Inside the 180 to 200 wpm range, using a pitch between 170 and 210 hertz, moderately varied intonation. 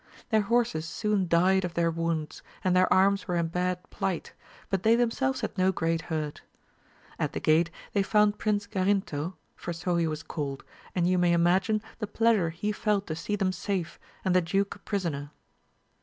Yes: average, 185 wpm; medium, 185 Hz; average, 3.4 semitones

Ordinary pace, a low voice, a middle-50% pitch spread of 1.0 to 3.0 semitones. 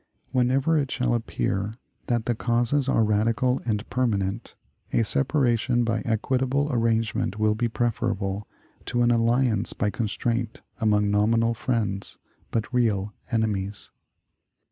No: slow, 120 wpm; low, 115 Hz; narrow, 2.5 semitones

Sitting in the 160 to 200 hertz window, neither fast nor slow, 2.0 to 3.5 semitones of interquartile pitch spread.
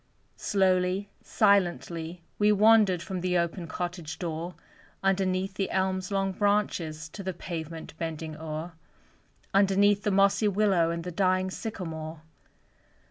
No: medium, 185 Hz; slow, 125 wpm; average, 2.8 semitones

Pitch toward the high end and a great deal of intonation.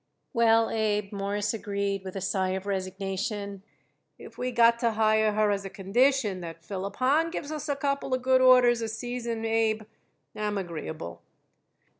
No: high, 215 Hz; average, 3.4 semitones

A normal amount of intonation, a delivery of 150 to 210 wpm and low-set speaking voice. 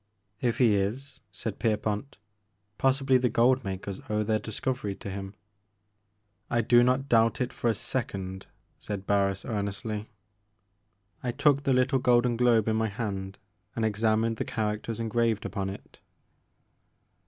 No: average, 3.3 semitones; average, 140 wpm; low, 110 Hz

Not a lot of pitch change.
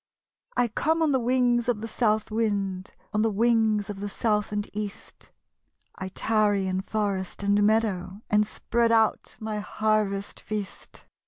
Yes: narrow, 2.0 semitones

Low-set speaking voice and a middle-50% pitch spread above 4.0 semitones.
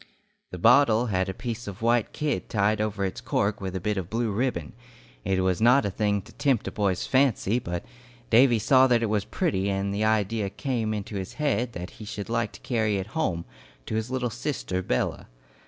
No: low, 110 Hz; average, 3.7 semitones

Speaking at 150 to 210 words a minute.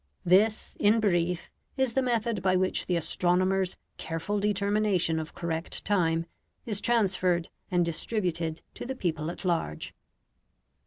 No: slow, 135 wpm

